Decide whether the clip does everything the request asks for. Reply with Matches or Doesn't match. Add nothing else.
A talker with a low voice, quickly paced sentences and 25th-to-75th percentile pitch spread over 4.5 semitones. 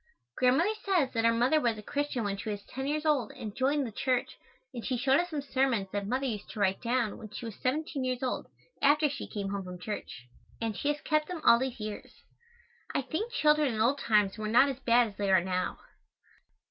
Doesn't match